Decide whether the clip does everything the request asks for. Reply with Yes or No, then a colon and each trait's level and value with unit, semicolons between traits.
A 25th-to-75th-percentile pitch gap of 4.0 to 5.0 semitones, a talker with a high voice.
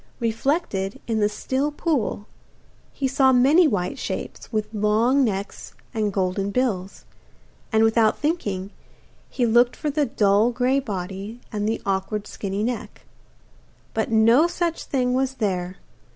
Yes: average, 4.6 semitones; high, 225 Hz